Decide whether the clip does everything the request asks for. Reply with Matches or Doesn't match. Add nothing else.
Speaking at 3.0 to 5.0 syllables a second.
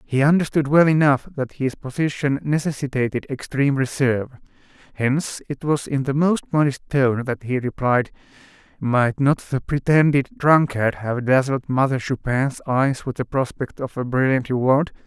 Matches